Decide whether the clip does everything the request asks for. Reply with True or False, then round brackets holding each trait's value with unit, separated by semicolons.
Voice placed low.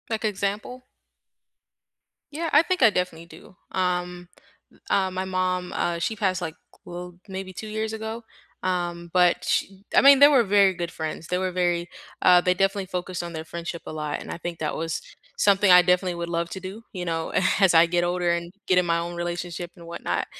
False (180 Hz)